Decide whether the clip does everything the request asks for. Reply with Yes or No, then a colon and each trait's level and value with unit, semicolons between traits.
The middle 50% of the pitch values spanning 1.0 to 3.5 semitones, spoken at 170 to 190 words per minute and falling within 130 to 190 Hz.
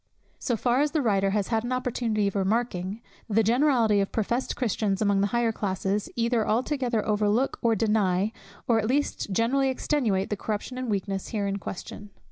No: average, 3.2 semitones; average, 180 wpm; high, 220 Hz